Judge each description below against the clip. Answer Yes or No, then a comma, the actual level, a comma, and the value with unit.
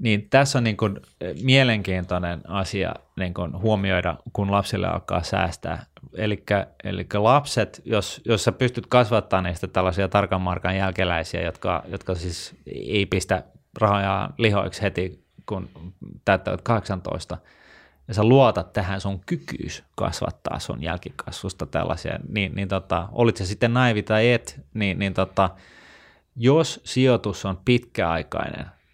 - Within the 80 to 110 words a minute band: No, average, 130 wpm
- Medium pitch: No, low, 100 Hz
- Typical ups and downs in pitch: Yes, average, 3.3 semitones